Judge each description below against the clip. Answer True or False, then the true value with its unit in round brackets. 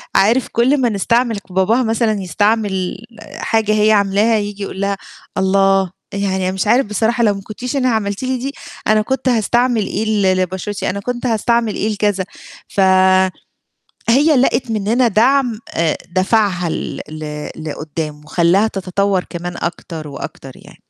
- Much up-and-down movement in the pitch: False (3.5 semitones)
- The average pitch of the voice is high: True (205 Hz)